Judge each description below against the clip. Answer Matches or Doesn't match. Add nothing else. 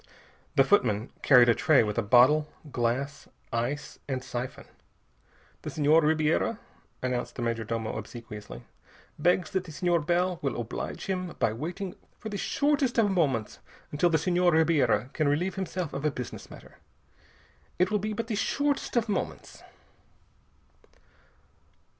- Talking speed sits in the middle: Matches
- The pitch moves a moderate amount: Doesn't match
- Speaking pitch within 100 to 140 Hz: Doesn't match